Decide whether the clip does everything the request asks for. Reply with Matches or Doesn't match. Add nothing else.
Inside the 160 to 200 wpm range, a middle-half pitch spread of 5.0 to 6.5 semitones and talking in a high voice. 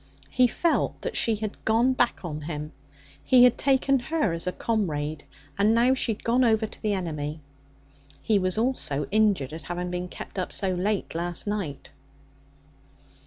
Matches